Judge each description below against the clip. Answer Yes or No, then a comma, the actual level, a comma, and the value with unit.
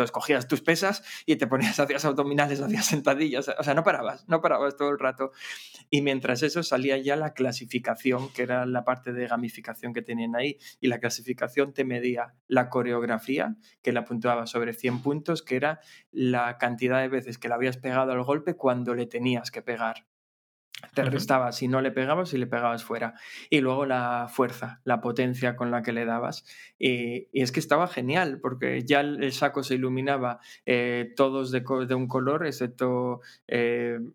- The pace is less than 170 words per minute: No, fast, 190 wpm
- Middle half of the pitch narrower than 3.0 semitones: Yes, narrow, 2.6 semitones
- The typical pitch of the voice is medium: No, low, 130 Hz